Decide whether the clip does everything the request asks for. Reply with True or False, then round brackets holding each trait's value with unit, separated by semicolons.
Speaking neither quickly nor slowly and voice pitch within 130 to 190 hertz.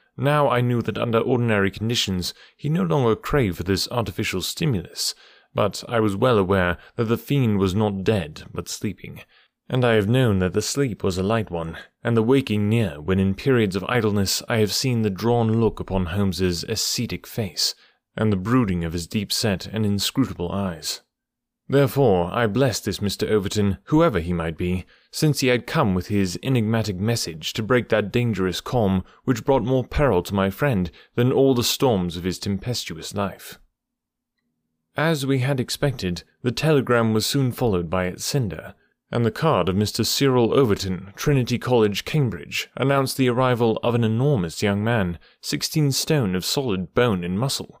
False (180 wpm; 110 Hz)